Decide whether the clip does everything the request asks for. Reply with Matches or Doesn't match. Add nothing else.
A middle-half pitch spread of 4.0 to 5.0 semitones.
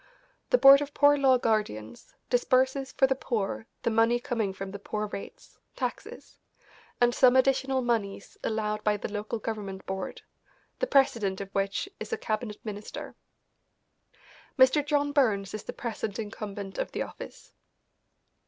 Matches